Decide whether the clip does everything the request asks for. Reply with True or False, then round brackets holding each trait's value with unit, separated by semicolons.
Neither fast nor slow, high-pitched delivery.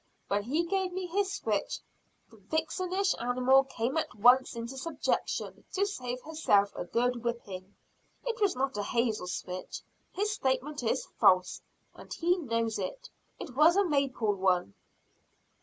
True (150 wpm; 260 Hz)